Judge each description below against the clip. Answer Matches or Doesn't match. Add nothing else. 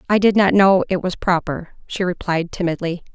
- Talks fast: Doesn't match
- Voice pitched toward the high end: Doesn't match